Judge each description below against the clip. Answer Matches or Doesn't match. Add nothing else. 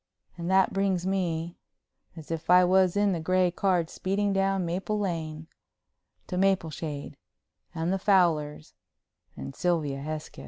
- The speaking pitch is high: Doesn't match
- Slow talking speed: Matches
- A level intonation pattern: Doesn't match